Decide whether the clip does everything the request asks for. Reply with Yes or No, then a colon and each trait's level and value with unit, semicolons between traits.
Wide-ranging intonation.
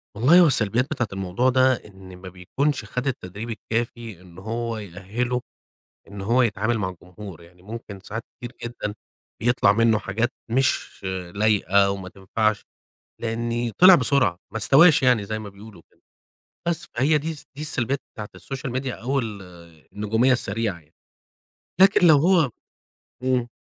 No: average, 4.3 semitones